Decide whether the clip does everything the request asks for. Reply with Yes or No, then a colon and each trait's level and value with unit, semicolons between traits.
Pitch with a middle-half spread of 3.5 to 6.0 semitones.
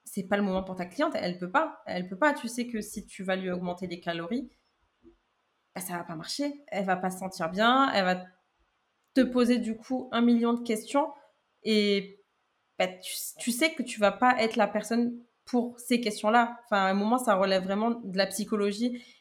Yes: average, 4.2 semitones